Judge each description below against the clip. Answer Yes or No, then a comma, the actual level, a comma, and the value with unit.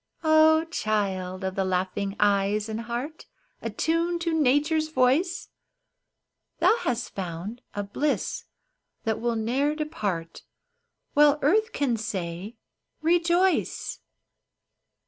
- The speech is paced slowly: Yes, slow, 105 wpm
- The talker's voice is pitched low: No, high, 240 Hz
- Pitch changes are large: Yes, wide, 7.7 semitones